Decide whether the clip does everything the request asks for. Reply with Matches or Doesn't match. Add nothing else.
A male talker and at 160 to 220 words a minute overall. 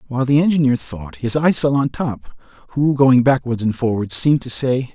Matches